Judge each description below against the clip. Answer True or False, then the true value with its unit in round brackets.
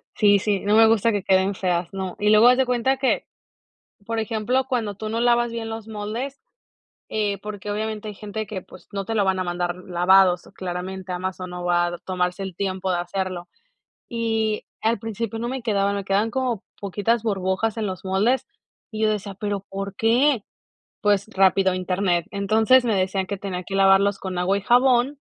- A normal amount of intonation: True (3.0 semitones)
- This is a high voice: True (200 Hz)